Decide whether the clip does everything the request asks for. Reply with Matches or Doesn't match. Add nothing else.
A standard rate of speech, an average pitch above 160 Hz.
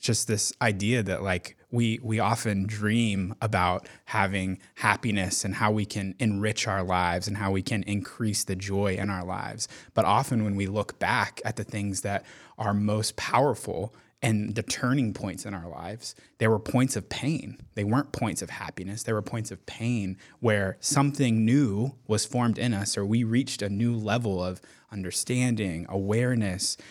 Doesn't match